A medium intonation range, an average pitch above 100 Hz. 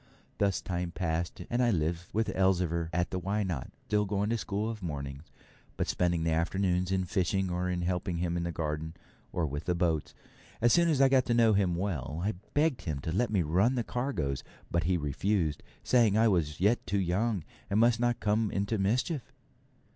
No: average, 4.2 semitones; very low, 95 Hz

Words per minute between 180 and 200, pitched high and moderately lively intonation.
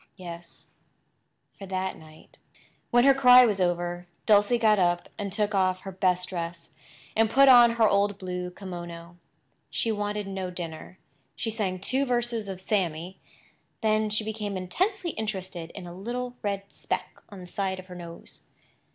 No: average, 160 wpm; high, 195 Hz; average, 3.4 semitones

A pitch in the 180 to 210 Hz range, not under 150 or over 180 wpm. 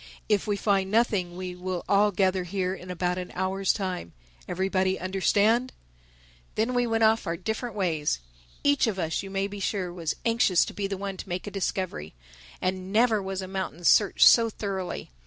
No: high, 190 Hz; average, 190 wpm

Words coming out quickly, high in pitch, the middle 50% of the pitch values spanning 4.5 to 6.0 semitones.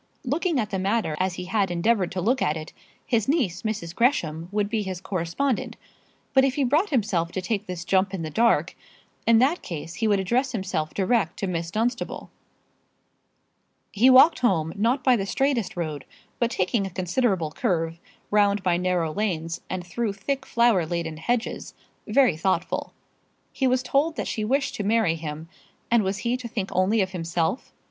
No: average, 185 wpm; high, 200 Hz; wide, 5.5 semitones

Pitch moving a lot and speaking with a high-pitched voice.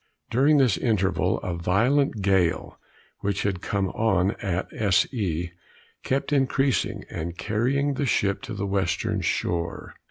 No: wide, 5.8 semitones; low, 100 Hz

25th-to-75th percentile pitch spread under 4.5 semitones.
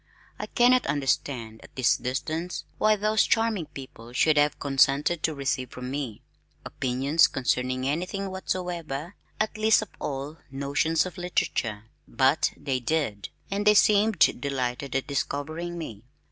No: average, 5.1 semitones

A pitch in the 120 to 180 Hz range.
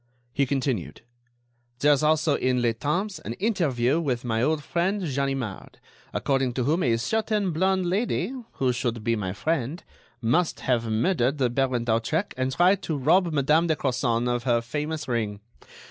Yes: low, 135 Hz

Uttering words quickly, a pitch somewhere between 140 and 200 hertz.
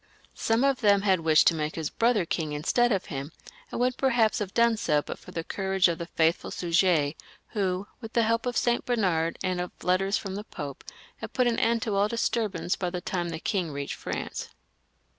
Yes: fast, 215 wpm; high, 190 Hz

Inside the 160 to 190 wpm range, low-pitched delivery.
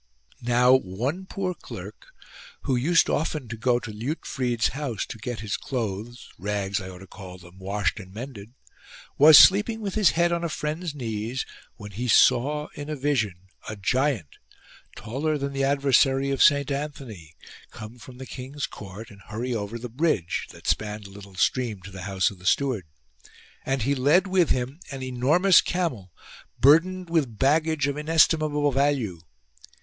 Yes: average, 170 wpm; low, 130 Hz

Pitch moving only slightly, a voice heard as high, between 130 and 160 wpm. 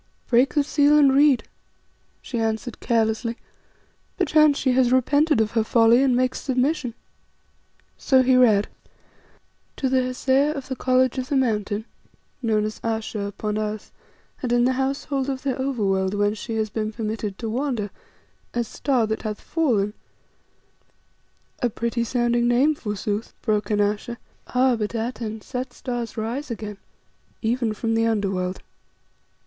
No: average, 3.2 semitones; high, 235 Hz; average, 155 wpm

